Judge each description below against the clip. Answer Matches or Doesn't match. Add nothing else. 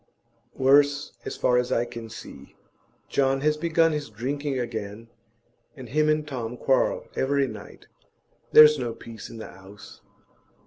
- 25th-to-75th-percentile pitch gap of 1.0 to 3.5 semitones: Doesn't match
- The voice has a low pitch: Matches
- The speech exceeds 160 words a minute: Doesn't match